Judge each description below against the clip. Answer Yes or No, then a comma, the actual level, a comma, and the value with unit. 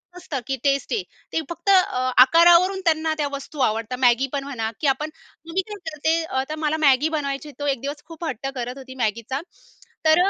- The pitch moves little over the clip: No, average, 3.5 semitones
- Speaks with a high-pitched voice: Yes, very high, 285 Hz